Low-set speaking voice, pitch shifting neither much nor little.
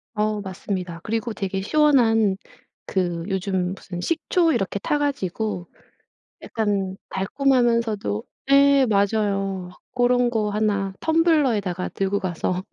No: high, 205 Hz; average, 4.2 semitones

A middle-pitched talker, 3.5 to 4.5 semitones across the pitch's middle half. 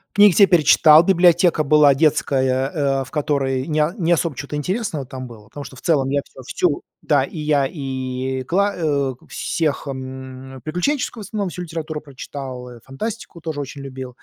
Yes: medium, 145 Hz; average, 3.9 semitones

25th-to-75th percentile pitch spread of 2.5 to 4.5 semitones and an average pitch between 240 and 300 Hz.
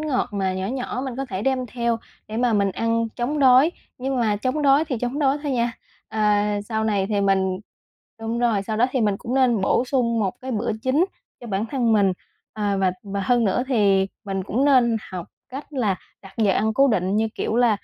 No: average, 4.0 semitones; high, 230 Hz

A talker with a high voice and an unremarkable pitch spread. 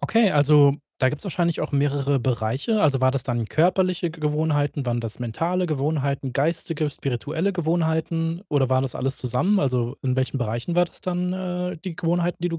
No: medium, 150 Hz; average, 4.6 semitones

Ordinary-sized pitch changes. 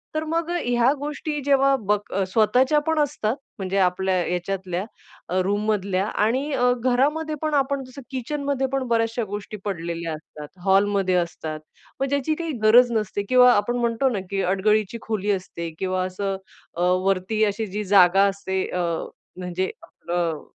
No: wide, 5.7 semitones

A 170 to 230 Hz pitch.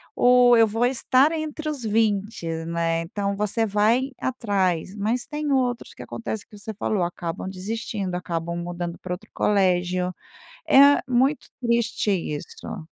Yes: high, 210 Hz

